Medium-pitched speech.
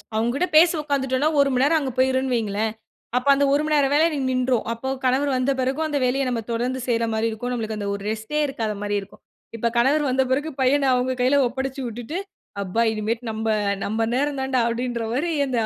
No: very high, 255 Hz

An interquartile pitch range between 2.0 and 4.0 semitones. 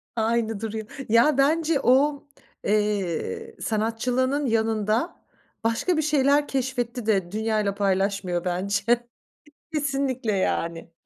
No: average, 4.9 semitones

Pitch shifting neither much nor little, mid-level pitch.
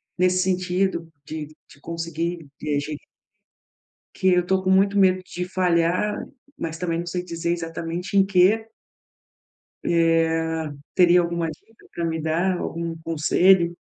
No: narrow, 2.0 semitones; medium, 170 Hz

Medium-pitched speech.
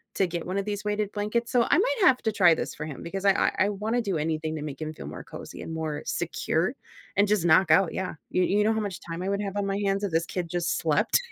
No: high, 195 Hz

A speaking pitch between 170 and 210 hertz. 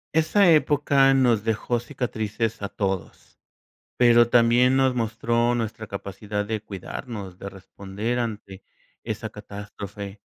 No: low, 115 Hz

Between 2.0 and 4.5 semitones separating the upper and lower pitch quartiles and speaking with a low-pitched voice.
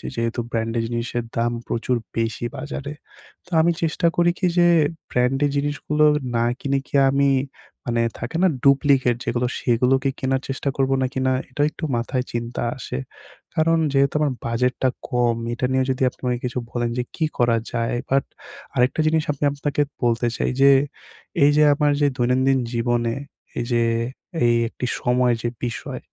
Yes: average, 2.9 semitones; low, 125 Hz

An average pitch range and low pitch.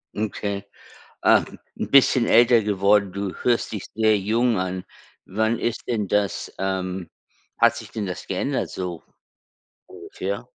Yes: average, 3.3 semitones; low, 105 Hz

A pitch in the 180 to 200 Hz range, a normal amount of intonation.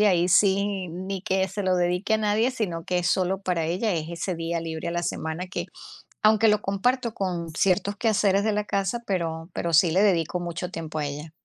Yes: medium, 185 Hz; average, 3.1 semitones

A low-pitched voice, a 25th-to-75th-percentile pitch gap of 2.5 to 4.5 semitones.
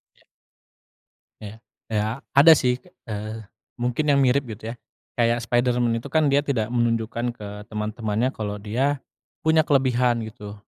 Yes: low, 120 Hz; average, 3.1 semitones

